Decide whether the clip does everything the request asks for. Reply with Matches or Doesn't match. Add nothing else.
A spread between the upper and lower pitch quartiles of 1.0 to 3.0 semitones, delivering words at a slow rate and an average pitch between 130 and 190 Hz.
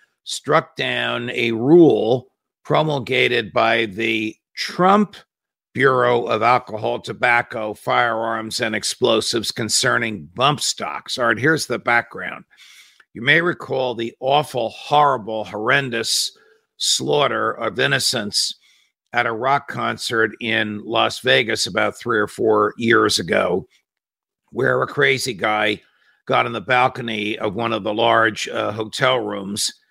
Doesn't match